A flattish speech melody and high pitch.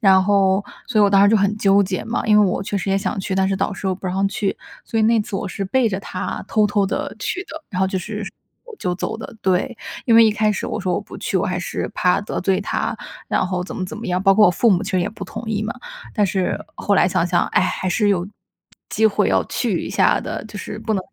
Yes: narrow, 2.1 semitones; high, 200 Hz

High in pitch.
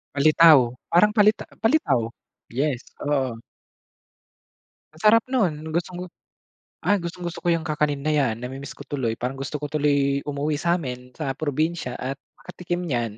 No: medium, 150 Hz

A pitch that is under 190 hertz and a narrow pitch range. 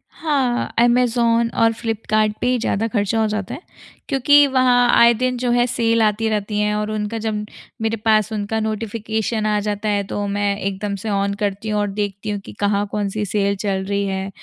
No: high, 215 Hz; narrow, 2.1 semitones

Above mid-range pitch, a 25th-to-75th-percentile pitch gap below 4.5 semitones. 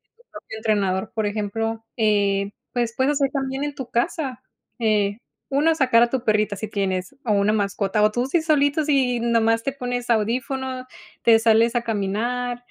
Yes: high, 230 Hz; average, 3.7 semitones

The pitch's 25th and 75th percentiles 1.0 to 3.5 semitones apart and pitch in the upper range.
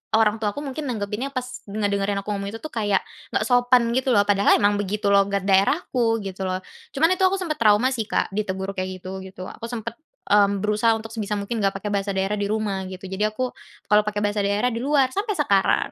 Yes: average, 3.1 semitones; high, 210 Hz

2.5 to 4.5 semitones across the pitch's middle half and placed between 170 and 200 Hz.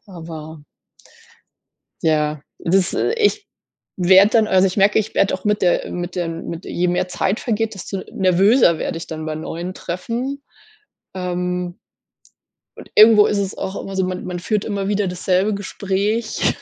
Yes: average, 2.9 semitones; high, 190 Hz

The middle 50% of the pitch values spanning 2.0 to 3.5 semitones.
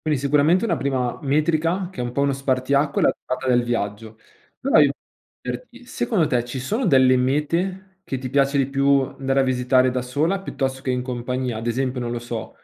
Yes: average, 2.9 semitones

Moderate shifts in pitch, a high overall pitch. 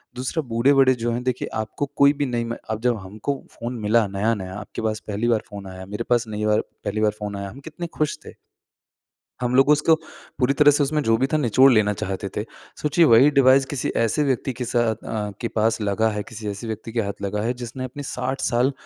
No: average, 3.7 semitones; low, 115 Hz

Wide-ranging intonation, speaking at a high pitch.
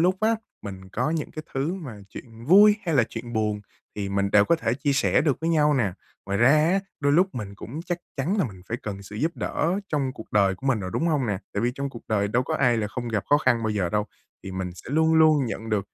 No: wide, 6.8 semitones; low, 125 Hz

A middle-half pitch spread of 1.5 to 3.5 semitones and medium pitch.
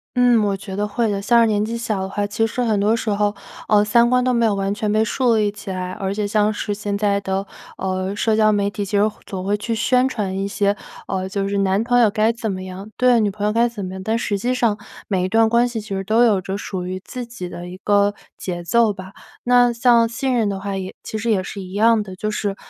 No: average, 2.7 semitones; high, 210 Hz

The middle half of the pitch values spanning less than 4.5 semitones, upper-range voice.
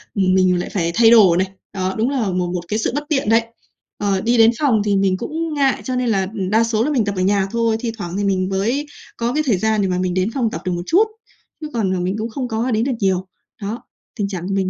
Yes: average, 3.9 semitones; high, 210 Hz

